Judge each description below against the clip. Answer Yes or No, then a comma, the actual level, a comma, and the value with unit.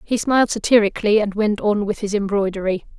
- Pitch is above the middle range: Yes, high, 205 Hz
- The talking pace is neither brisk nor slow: Yes, average, 180 wpm